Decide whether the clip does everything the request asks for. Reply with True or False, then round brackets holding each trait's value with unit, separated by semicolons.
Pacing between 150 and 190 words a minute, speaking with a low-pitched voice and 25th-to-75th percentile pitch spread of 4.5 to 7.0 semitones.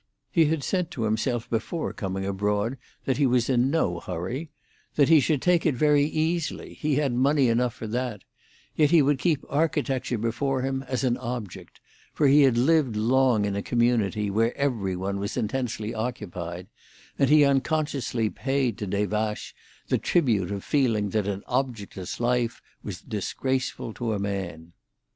True (165 wpm; 125 Hz; 4.9 semitones)